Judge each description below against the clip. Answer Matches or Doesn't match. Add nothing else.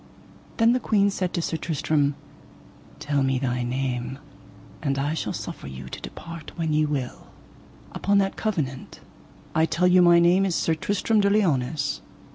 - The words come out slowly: Doesn't match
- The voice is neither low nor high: Matches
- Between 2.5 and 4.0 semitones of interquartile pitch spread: Doesn't match